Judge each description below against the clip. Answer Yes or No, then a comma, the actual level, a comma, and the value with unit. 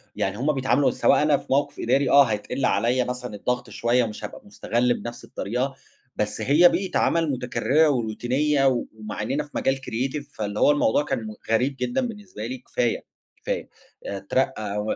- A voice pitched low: Yes, low, 125 Hz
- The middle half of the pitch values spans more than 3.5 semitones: Yes, average, 3.9 semitones